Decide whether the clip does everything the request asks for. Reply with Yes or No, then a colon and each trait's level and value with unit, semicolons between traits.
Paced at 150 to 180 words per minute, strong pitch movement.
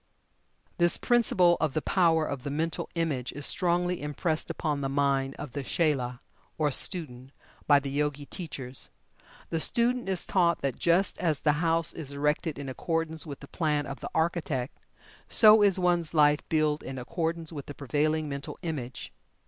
No: average, 170 wpm; average, 3.2 semitones